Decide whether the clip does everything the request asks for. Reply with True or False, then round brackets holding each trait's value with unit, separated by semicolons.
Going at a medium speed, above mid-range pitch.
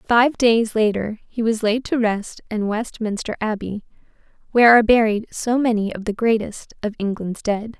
True (170 wpm; 220 Hz)